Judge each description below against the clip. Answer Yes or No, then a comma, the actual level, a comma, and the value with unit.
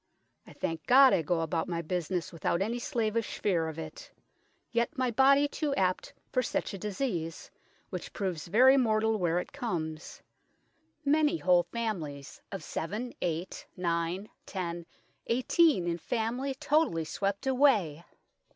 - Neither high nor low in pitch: No, high, 200 Hz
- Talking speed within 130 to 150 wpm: Yes, average, 140 wpm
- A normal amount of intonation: No, wide, 6.9 semitones